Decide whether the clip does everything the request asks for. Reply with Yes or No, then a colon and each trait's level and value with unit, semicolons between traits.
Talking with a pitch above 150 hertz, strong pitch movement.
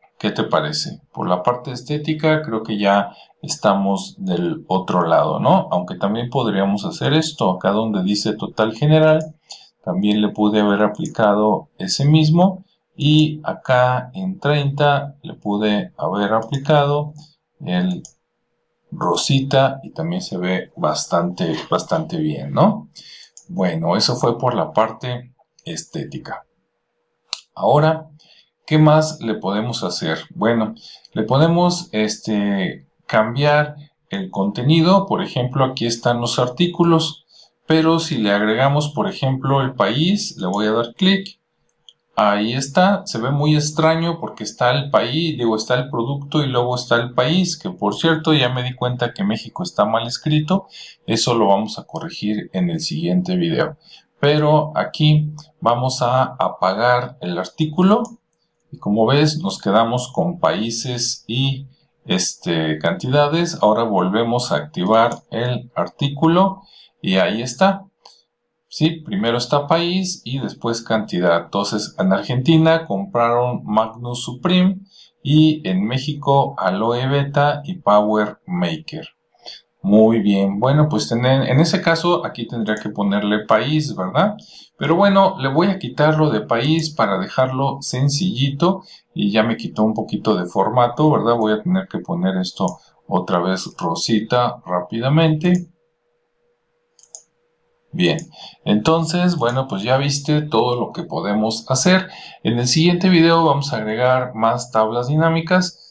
No: medium, 140 Hz; wide, 6.1 semitones